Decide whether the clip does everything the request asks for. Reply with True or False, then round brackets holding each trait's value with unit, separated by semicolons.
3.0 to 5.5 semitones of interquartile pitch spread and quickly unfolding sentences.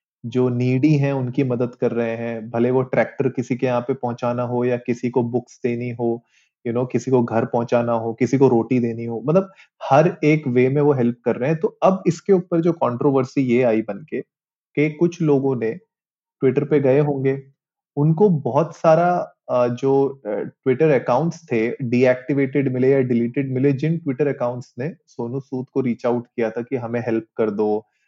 True (3.3 semitones; 200 wpm)